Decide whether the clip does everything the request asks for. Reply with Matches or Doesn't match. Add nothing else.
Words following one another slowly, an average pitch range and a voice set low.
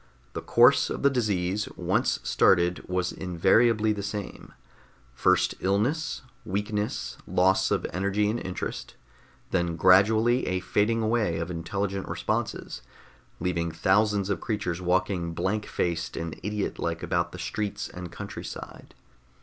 Matches